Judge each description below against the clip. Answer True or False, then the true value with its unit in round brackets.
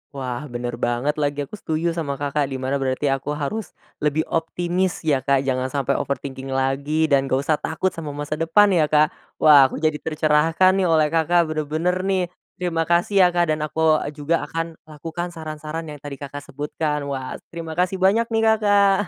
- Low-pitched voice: False (155 Hz)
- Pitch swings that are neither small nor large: True (3.3 semitones)